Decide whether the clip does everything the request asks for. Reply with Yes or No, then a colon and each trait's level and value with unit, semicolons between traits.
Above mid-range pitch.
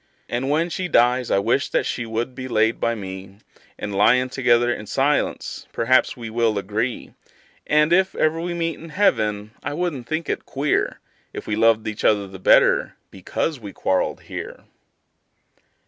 No: low, 120 Hz